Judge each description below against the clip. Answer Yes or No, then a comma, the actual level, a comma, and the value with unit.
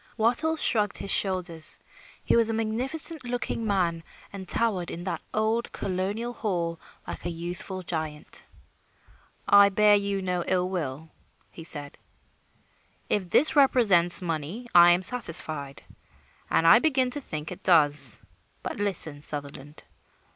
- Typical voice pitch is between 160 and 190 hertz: Yes, medium, 185 Hz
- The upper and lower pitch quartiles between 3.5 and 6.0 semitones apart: Yes, average, 5.0 semitones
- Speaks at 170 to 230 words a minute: No, slow, 135 wpm